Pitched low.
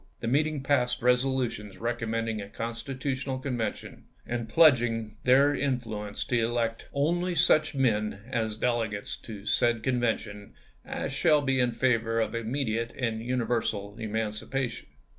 Yes: low, 120 Hz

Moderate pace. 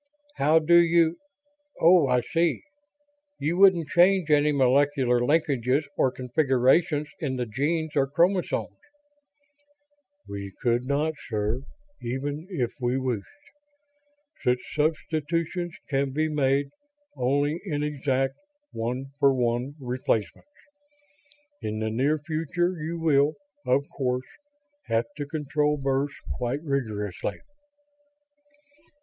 No: slow, 110 wpm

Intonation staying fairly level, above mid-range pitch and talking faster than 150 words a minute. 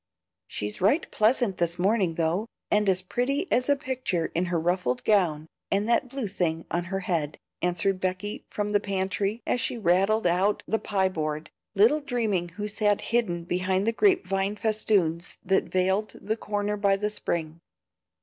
No: average, 3.4 semitones; high, 195 Hz; average, 170 wpm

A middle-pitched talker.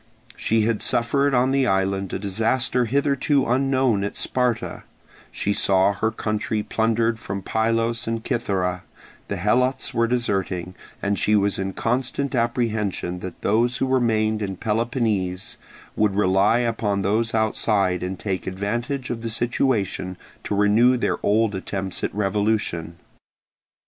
No: low, 110 Hz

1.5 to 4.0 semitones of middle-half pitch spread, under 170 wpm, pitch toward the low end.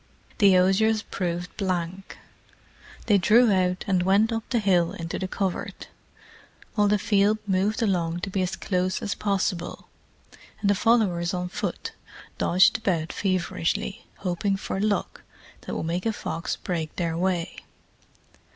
No: narrow, 2.5 semitones; average, 145 wpm; high, 190 Hz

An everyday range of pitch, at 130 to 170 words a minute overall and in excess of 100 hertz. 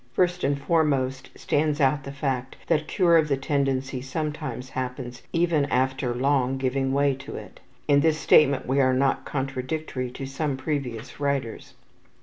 No: narrow, 2.2 semitones; average, 155 wpm; low, 135 Hz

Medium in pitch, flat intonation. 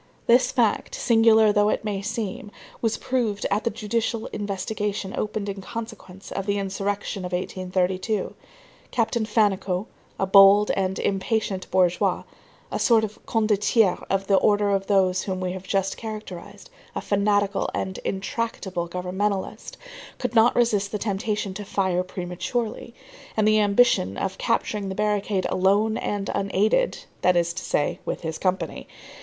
No: high, 200 Hz; narrow, 2.3 semitones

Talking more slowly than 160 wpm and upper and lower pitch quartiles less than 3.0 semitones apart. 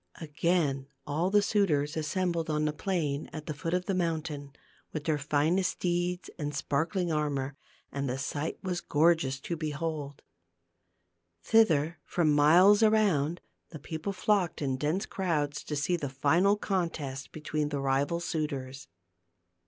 No: average, 145 wpm; average, 3.4 semitones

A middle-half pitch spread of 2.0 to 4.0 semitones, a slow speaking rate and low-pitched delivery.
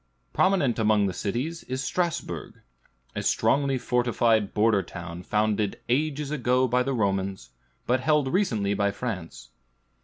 No: average, 5.1 semitones; slow, 130 wpm; low, 120 Hz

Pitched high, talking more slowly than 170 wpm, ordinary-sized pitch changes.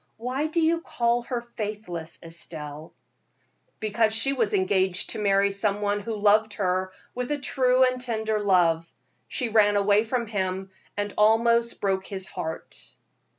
Yes: high, 210 Hz; average, 150 wpm; average, 3.6 semitones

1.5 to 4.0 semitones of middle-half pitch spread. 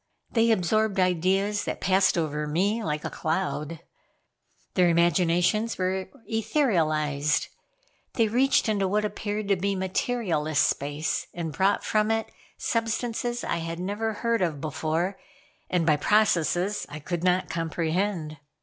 No: average, 4.6 semitones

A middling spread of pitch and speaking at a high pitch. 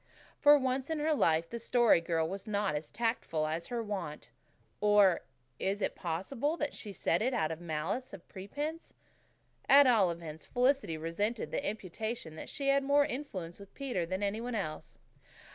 No: wide, 7.4 semitones; high, 205 Hz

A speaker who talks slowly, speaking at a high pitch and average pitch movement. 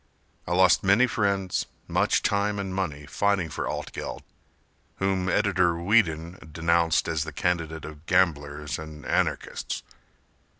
No: slow, 125 wpm; very low, 85 Hz; average, 3.5 semitones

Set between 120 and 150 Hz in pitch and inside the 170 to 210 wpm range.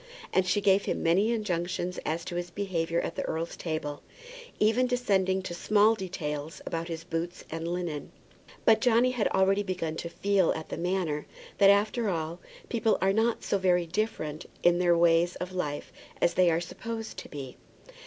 No: medium, 180 Hz; average, 180 wpm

